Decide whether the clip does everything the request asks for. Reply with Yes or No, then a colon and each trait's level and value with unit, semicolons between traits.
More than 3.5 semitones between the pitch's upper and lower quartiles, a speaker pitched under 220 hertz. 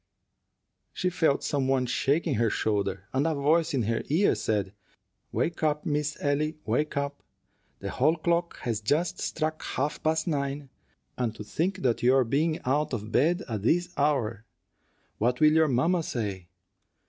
Yes: average, 4.9 semitones; medium, 140 Hz